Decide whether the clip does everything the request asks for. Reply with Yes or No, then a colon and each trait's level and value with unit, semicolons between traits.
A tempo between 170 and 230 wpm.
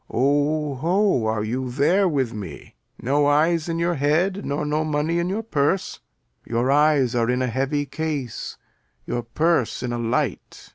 Yes: average, 175 wpm